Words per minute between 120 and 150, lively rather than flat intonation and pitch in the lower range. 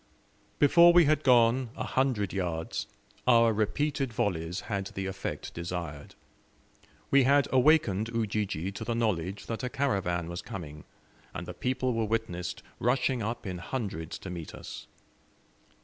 Yes: average, 145 wpm; wide, 6.1 semitones; low, 110 Hz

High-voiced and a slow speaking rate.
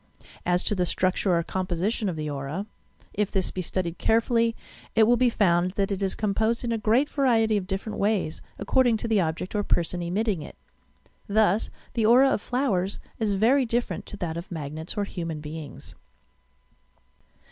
No: high, 200 Hz; average, 180 wpm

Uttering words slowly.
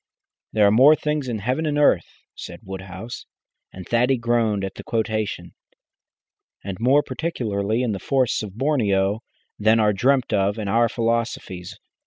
No: average, 155 wpm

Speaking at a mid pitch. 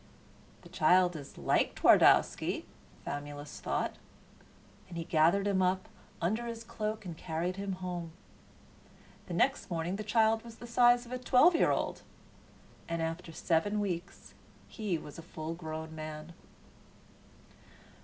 Yes: medium, 180 Hz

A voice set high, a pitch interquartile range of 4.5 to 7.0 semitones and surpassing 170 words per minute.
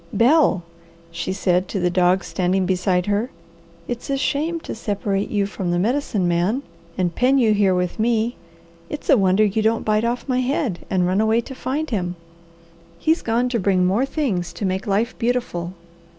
Yes: high, 205 Hz; average, 5.0 semitones; average, 185 wpm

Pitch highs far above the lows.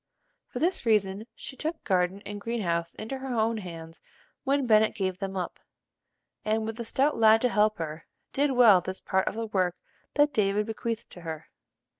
No: average, 3.9 semitones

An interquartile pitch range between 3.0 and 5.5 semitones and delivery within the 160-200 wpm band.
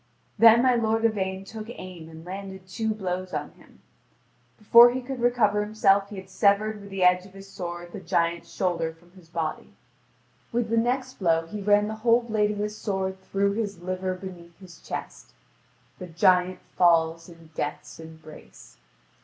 Yes: average, 3.6 semitones; average, 175 wpm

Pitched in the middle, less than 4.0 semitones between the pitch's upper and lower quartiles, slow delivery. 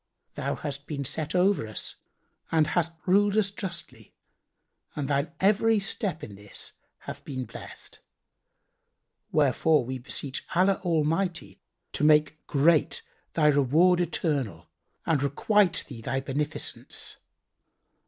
No: medium, 155 Hz; average, 4.5 semitones; slow, 120 wpm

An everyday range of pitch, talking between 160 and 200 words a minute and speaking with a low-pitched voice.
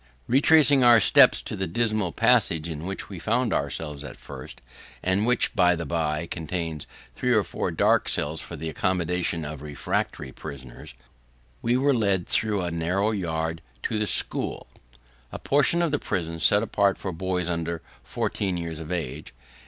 Yes: average, 4.5 semitones; average, 170 wpm; very low, 90 Hz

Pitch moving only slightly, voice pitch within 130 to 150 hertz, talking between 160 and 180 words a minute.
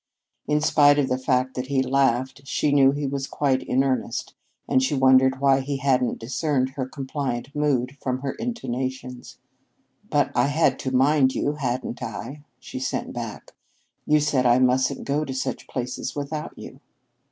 Yes: narrow, 1.8 semitones; low, 135 Hz; average, 170 wpm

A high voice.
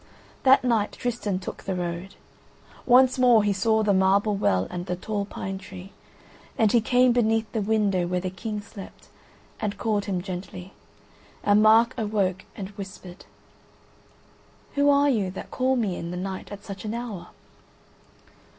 Yes: high, 205 Hz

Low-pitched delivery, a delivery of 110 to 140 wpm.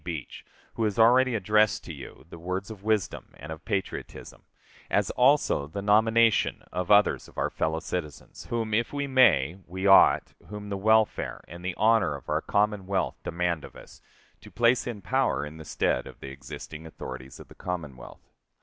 No: low, 100 Hz; average, 180 wpm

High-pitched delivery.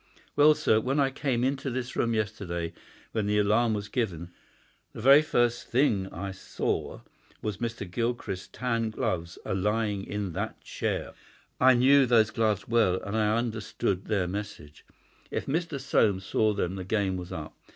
No: low, 110 Hz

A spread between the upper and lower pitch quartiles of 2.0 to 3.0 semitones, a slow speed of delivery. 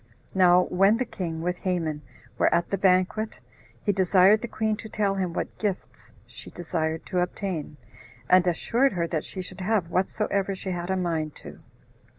No: narrow, 2.4 semitones; average, 175 wpm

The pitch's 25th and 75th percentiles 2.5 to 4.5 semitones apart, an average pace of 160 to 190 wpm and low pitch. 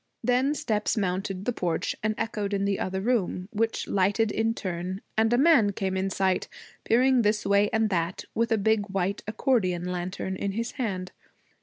No: average, 3.0 semitones; average, 180 wpm; high, 205 Hz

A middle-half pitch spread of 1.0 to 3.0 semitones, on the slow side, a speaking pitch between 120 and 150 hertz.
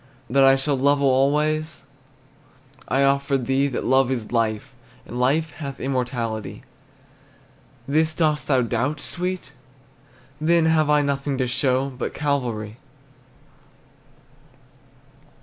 Yes: average, 2.7 semitones; slow, 115 wpm; low, 135 Hz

